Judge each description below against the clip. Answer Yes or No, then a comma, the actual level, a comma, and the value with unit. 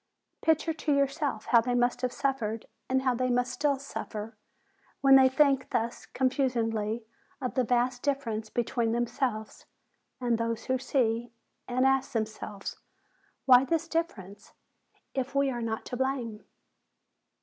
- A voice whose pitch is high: Yes, very high, 250 Hz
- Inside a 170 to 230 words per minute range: No, average, 140 wpm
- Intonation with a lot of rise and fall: No, average, 2.9 semitones